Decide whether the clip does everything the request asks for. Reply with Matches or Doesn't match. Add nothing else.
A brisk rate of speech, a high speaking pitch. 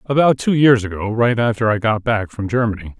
Doesn't match